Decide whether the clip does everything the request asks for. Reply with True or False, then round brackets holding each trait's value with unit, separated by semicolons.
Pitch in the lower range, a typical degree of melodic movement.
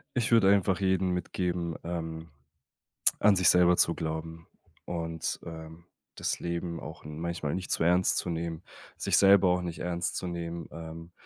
False (85 Hz; 1.6 semitones)